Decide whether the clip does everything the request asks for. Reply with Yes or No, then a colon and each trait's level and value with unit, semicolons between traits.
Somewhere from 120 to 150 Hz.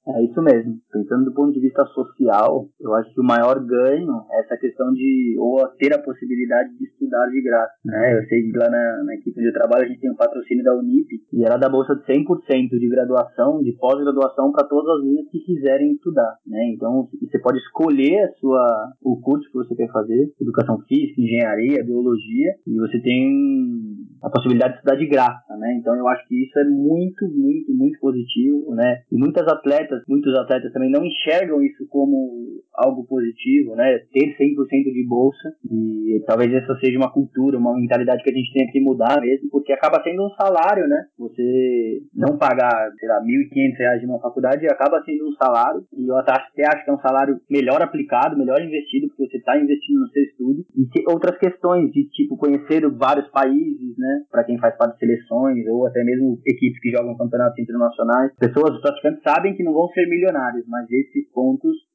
Yes: medium, 140 Hz